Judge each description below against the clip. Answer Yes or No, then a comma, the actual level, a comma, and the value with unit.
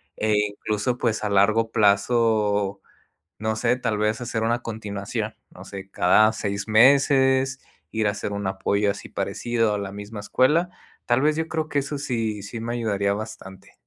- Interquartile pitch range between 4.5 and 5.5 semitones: No, average, 2.9 semitones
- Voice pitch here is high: No, low, 110 Hz